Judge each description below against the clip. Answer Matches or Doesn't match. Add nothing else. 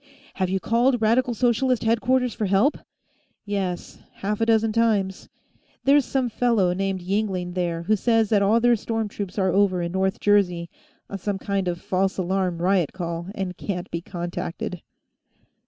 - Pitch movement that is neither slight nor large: Matches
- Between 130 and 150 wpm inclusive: Doesn't match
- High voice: Matches